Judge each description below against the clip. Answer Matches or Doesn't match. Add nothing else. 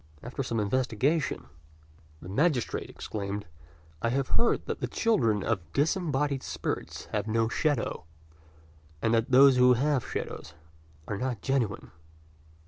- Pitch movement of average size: Matches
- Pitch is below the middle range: Matches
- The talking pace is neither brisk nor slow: Doesn't match